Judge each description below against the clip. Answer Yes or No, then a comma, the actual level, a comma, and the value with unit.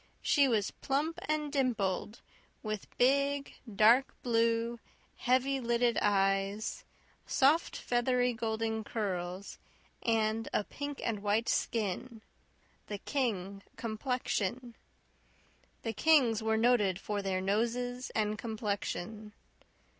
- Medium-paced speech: No, slow, 100 wpm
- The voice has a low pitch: No, high, 225 Hz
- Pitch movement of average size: Yes, average, 3.2 semitones